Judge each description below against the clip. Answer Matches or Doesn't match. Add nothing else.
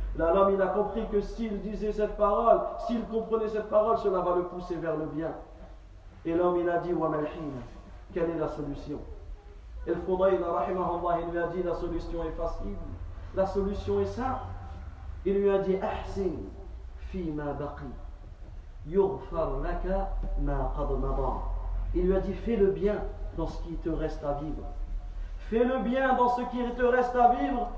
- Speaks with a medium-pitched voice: Matches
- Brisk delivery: Matches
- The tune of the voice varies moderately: Doesn't match